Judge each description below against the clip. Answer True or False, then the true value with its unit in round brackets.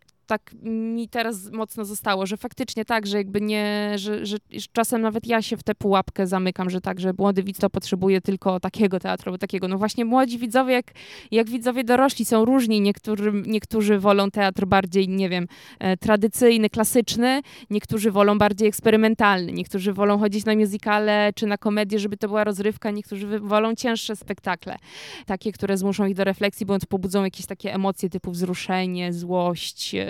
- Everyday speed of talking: False (170 wpm)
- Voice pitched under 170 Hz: False (210 Hz)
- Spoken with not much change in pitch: True (2.2 semitones)